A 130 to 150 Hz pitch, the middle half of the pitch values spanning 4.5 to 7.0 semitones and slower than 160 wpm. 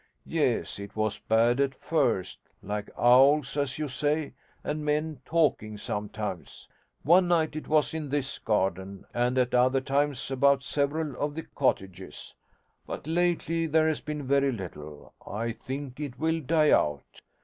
Yes: low, 135 Hz; wide, 5.4 semitones; average, 150 wpm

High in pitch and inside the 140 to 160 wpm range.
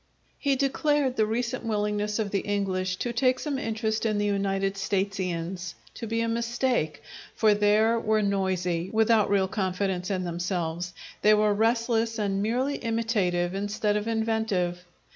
Yes: high, 210 Hz; average, 150 wpm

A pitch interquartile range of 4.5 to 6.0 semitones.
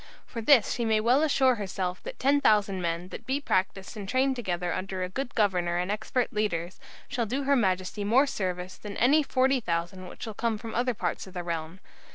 Yes: wide, 5.5 semitones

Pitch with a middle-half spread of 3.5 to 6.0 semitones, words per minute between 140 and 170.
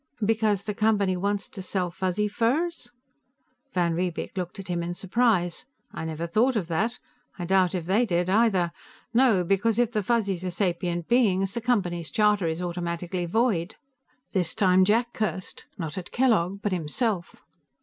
Yes: average, 3.9 semitones; average, 160 wpm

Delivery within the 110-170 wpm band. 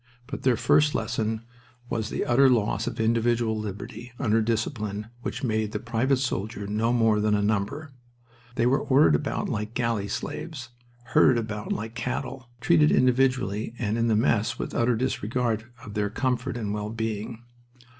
Yes: average, 165 wpm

